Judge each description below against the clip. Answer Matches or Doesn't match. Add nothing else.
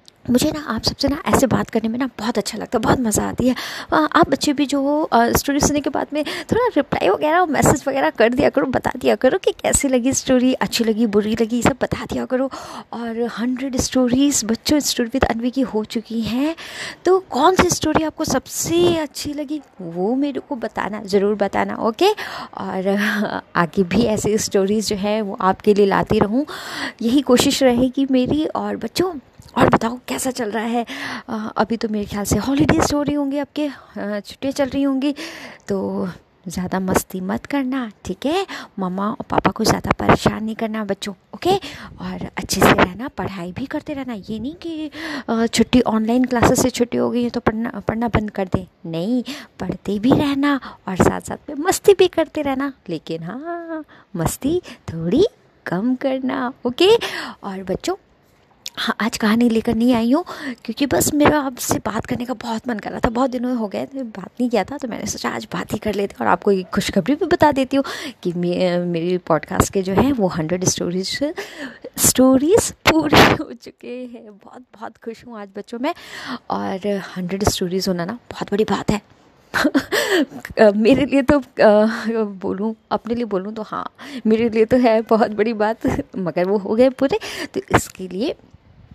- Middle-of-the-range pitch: Doesn't match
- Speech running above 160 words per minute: Matches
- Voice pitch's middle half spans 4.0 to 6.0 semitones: Matches